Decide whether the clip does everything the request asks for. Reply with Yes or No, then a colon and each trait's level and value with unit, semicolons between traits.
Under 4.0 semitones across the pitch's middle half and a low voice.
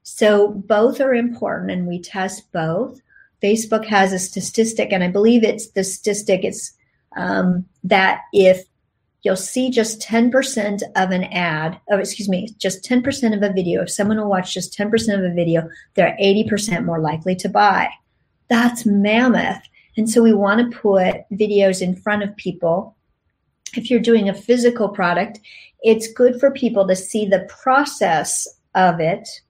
No: average, 3.3 semitones; high, 205 Hz